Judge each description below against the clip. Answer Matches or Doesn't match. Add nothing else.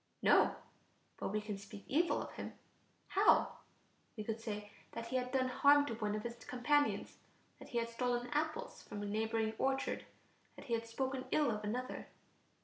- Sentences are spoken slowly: Doesn't match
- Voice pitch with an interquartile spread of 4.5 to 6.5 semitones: Doesn't match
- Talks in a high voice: Matches